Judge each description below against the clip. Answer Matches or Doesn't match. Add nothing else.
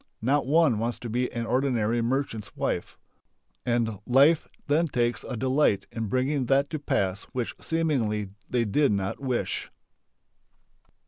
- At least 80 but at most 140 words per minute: Matches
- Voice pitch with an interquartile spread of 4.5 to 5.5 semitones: Doesn't match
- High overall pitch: Doesn't match